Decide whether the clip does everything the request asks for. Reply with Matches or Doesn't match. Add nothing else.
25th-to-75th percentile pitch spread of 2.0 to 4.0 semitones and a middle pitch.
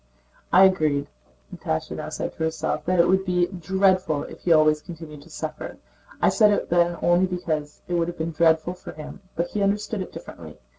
Matches